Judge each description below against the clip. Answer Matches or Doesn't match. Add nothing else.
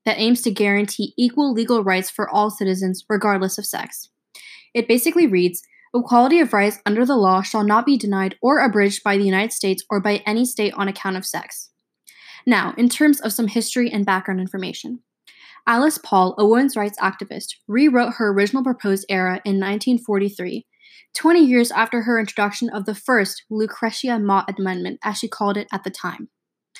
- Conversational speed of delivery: Matches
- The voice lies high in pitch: Matches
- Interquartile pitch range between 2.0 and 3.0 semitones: Doesn't match